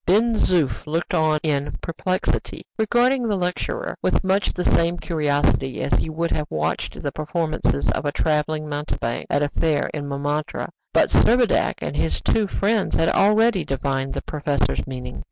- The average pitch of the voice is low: No, medium, 155 Hz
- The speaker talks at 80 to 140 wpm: No, average, 165 wpm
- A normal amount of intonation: Yes, average, 4.8 semitones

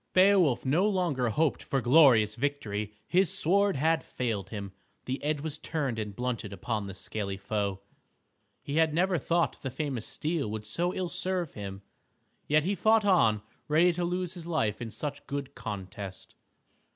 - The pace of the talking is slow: No, average, 165 wpm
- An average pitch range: No, wide, 8.1 semitones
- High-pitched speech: No, medium, 140 Hz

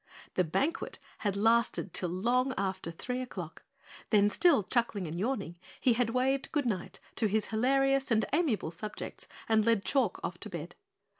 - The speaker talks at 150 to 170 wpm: Yes, average, 160 wpm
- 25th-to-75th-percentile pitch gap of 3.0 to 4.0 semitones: No, average, 4.8 semitones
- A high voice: Yes, high, 225 Hz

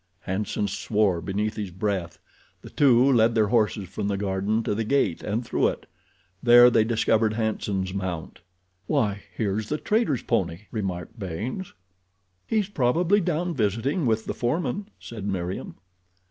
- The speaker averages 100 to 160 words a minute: Yes, average, 145 wpm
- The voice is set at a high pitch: No, low, 110 Hz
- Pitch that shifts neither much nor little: Yes, average, 3.9 semitones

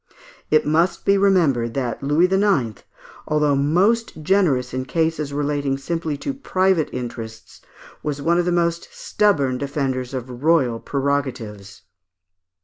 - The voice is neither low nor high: Yes, medium, 145 Hz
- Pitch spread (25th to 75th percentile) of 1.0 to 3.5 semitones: No, average, 4.8 semitones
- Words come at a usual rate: No, slow, 130 wpm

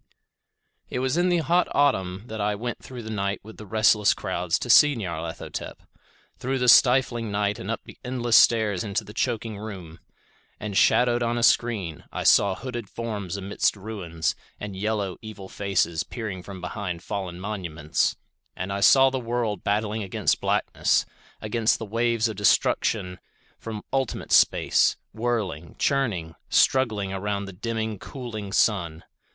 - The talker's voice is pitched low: Yes, low, 105 Hz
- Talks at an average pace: Yes, average, 155 wpm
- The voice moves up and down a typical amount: Yes, average, 3.6 semitones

